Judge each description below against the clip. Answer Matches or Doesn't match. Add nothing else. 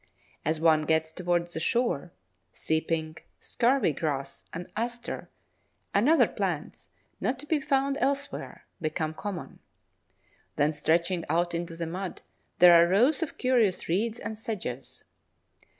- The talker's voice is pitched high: Doesn't match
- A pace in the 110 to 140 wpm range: Matches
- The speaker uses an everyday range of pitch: Doesn't match